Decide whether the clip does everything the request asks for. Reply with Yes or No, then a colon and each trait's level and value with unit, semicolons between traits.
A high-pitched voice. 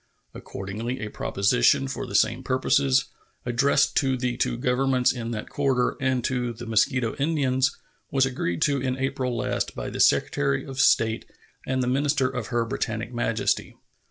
No: low, 125 Hz